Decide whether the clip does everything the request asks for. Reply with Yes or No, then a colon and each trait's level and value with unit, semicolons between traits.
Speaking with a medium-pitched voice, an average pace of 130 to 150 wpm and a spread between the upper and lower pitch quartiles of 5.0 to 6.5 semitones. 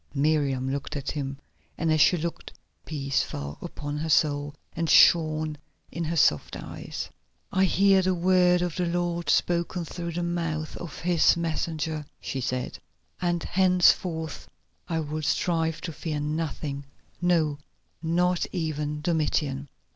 No: medium, 160 Hz; average, 140 wpm; average, 2.7 semitones